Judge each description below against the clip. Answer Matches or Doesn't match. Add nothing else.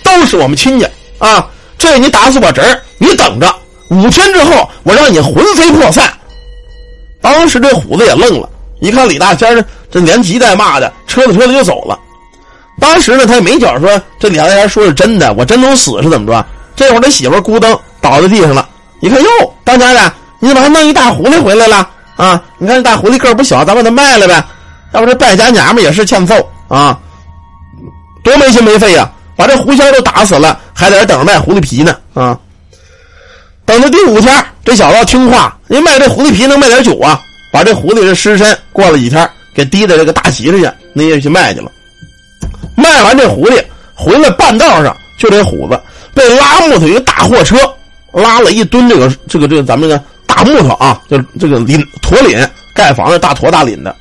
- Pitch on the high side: Matches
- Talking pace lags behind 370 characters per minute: Matches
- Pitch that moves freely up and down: Matches